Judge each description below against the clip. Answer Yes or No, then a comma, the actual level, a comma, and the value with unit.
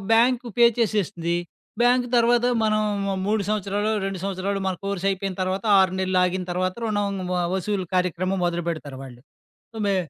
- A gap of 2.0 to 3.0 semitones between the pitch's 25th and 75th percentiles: Yes, narrow, 2.6 semitones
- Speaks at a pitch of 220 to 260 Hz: No, high, 195 Hz